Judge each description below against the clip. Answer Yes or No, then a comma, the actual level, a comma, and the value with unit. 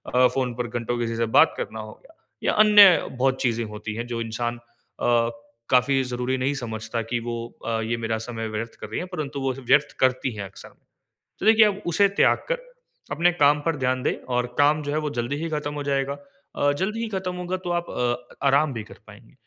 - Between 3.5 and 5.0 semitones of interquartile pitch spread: Yes, average, 4.2 semitones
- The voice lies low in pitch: Yes, low, 130 Hz